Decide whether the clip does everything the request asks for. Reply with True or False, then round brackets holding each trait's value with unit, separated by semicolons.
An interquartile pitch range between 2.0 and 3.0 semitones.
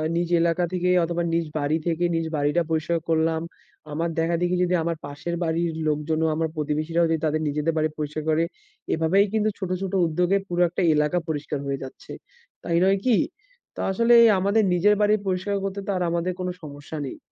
True (2.6 semitones)